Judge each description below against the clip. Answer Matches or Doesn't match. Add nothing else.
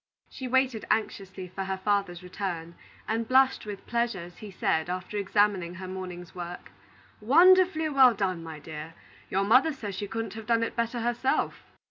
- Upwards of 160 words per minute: Matches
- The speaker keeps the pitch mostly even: Doesn't match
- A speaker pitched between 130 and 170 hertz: Doesn't match